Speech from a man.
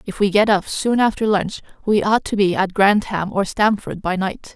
No: female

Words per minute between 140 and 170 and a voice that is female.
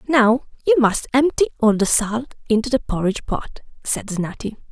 Yes: average, 165 wpm; female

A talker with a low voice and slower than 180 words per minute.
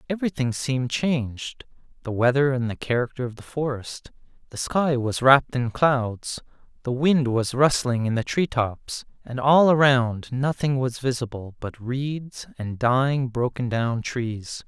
Yes: low, 130 Hz; average, 150 wpm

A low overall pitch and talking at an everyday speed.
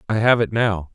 No: low, 105 Hz; fast, 255 wpm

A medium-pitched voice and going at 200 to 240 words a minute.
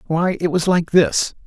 Yes: medium, 165 Hz; fast, 205 wpm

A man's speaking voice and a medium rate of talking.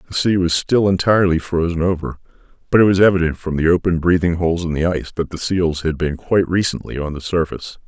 No: male; fast, 220 wpm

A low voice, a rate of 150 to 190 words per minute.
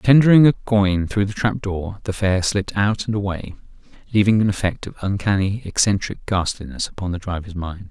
Yes: low, 100 Hz; average, 180 wpm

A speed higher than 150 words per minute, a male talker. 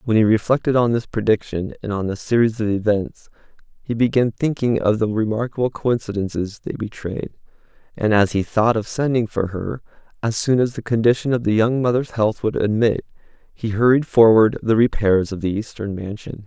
Yes: average, 180 wpm; male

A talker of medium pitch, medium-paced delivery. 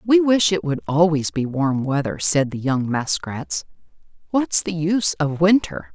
Yes: medium, 155 Hz; average, 170 wpm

